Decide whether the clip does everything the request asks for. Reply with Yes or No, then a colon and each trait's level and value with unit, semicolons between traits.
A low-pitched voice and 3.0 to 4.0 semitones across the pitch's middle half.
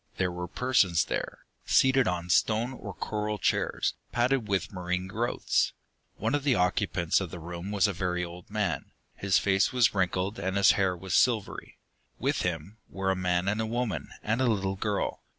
Yes: very low, 95 Hz; average, 3.5 semitones